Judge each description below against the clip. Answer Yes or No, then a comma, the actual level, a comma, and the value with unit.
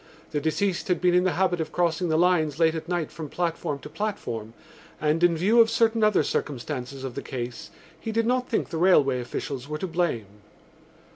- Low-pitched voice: No, medium, 165 Hz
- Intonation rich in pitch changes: No, average, 4.3 semitones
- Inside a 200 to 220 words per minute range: Yes, fast, 205 wpm